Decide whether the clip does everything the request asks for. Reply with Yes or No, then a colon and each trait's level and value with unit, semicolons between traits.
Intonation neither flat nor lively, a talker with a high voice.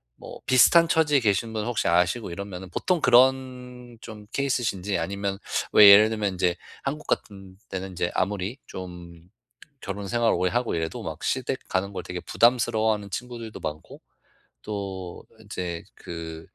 No: average, 4.7 semitones; low, 100 Hz